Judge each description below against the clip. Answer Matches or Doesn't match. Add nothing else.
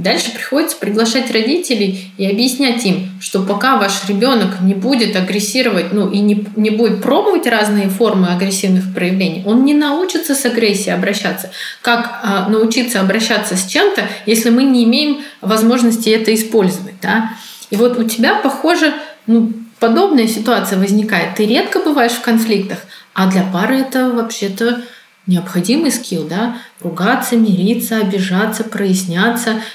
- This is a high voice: Matches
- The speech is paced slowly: Doesn't match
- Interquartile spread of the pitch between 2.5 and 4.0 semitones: Matches